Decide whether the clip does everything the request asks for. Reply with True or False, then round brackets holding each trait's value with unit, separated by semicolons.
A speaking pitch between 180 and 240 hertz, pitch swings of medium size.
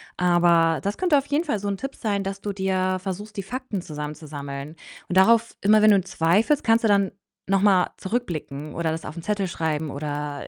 True (190 Hz; 4.7 semitones)